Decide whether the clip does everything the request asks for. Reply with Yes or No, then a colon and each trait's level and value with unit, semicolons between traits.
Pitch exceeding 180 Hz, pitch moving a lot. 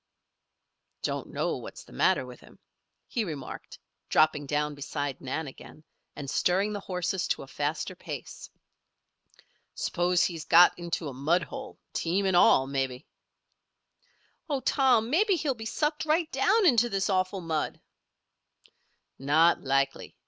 No: medium, 175 Hz; wide, 7.2 semitones